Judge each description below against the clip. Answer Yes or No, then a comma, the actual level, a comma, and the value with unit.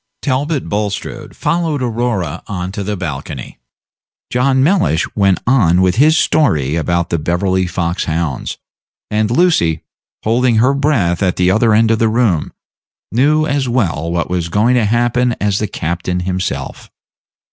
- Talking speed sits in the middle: Yes, average, 150 wpm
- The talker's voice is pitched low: Yes, low, 105 Hz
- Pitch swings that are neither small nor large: No, wide, 6.2 semitones